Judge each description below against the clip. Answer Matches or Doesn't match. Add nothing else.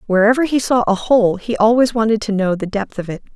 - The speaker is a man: Doesn't match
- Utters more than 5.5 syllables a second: Matches